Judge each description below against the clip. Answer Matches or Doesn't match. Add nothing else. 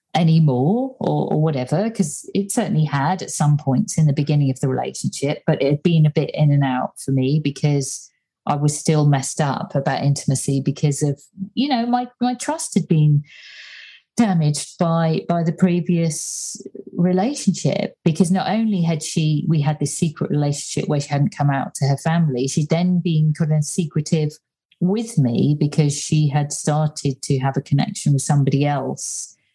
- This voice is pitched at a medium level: Matches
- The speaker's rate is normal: Matches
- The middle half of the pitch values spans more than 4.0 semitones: Doesn't match